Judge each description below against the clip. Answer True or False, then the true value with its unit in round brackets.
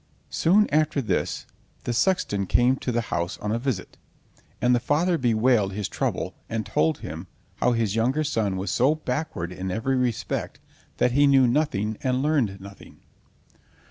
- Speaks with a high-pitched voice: False (120 Hz)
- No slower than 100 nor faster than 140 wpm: False (165 wpm)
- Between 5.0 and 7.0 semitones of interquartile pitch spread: True (5.3 semitones)